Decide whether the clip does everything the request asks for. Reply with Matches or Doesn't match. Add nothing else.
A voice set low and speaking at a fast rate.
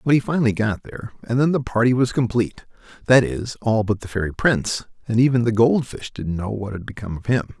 Matches